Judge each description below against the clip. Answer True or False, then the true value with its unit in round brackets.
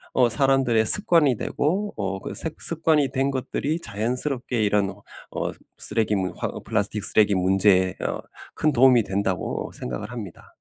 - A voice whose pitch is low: True (115 Hz)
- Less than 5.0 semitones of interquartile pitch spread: False (5.3 semitones)